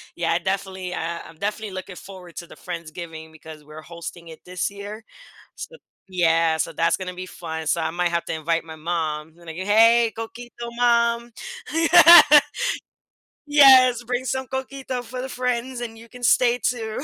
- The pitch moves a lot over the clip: Yes, wide, 6.3 semitones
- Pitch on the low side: No, high, 190 Hz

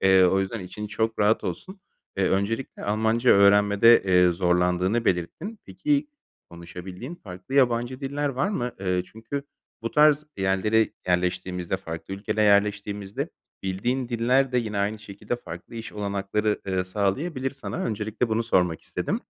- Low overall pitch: Yes, low, 105 Hz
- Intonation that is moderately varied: Yes, average, 4.2 semitones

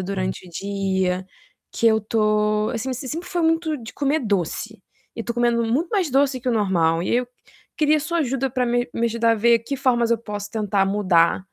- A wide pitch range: No, average, 4.6 semitones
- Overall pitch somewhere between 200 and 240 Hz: Yes, high, 230 Hz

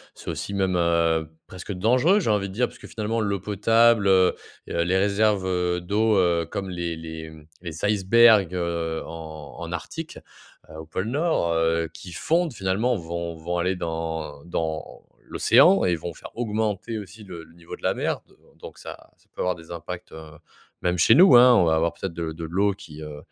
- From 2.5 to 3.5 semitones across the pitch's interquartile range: No, average, 4.3 semitones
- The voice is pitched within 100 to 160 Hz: No, very low, 90 Hz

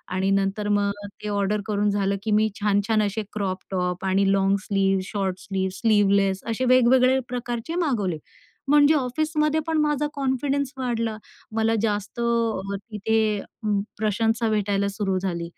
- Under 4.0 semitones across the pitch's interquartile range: Yes, average, 3.5 semitones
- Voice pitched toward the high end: Yes, high, 210 Hz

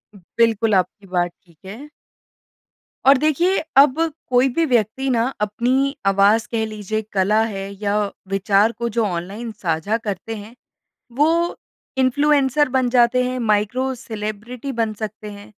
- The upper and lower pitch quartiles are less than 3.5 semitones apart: No, average, 3.9 semitones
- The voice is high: Yes, high, 225 Hz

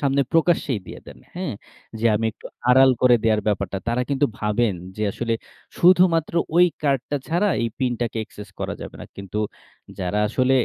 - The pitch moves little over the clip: No, average, 5.1 semitones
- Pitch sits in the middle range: No, low, 125 Hz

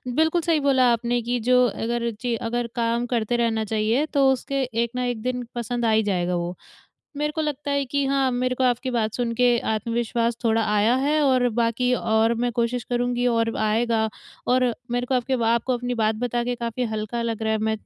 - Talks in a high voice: Yes, high, 240 Hz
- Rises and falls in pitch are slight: Yes, narrow, 1.9 semitones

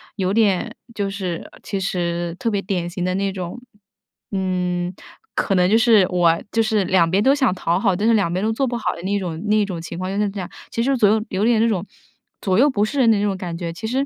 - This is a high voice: Yes, high, 195 Hz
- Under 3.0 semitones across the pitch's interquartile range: No, average, 3.5 semitones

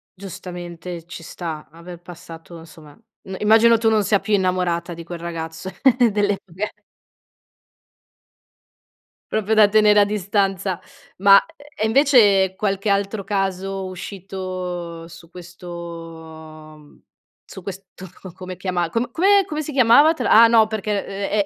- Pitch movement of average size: Yes, average, 3.6 semitones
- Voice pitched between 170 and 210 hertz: Yes, high, 190 Hz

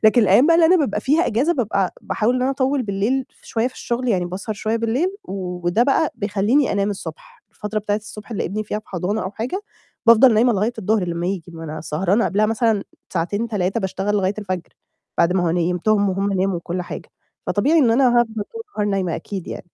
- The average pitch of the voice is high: Yes, high, 210 Hz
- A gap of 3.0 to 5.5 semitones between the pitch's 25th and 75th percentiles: Yes, average, 4.0 semitones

